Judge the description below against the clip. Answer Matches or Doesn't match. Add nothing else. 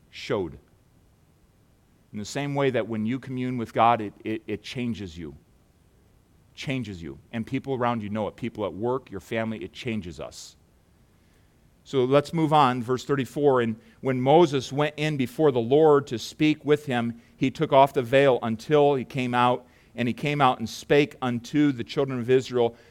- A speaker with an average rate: Matches